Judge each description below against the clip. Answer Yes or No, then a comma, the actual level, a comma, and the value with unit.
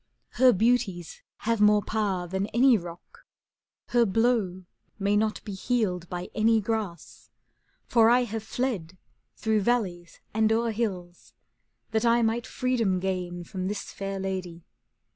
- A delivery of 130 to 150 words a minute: Yes, average, 145 wpm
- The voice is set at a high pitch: Yes, high, 210 Hz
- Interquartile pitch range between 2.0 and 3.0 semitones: No, average, 3.9 semitones